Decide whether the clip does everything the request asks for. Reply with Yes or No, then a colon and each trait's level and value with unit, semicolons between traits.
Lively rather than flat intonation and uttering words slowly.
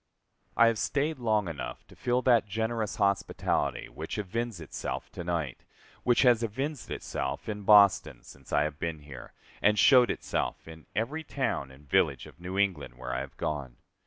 No: wide, 7.5 semitones; average, 175 wpm